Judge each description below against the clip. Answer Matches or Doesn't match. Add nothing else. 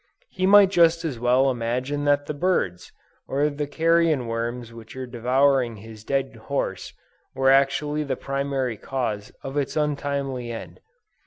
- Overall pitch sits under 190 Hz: Matches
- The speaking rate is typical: Matches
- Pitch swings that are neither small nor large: Matches